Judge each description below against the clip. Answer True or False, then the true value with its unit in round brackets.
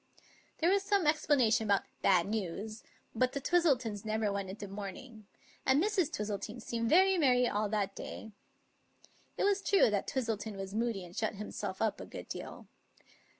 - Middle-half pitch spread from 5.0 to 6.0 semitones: True (5.5 semitones)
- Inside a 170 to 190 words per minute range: True (175 wpm)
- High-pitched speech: True (220 Hz)